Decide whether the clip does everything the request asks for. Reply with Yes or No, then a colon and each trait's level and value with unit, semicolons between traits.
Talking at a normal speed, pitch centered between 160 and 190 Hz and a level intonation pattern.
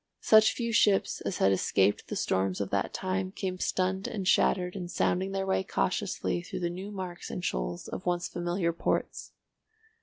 Yes: average, 180 wpm; medium, 185 Hz; narrow, 1.8 semitones